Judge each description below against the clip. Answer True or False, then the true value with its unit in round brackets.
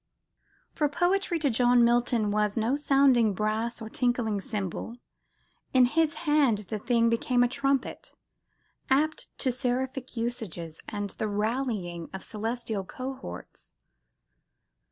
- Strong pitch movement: False (3.8 semitones)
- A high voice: True (240 Hz)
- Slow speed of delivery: True (120 wpm)